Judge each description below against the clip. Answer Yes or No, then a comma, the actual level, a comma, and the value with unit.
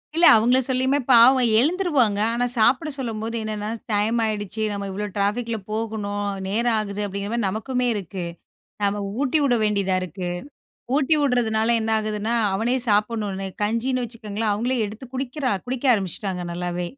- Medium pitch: No, high, 220 Hz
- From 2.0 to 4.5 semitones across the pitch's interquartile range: Yes, average, 3.3 semitones